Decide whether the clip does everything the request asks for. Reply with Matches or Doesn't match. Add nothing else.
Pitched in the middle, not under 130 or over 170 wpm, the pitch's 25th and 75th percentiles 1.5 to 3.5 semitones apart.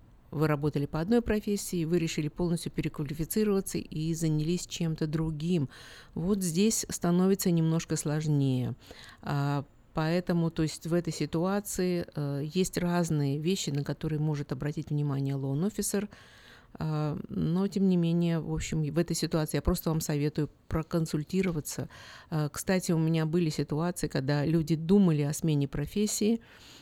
Matches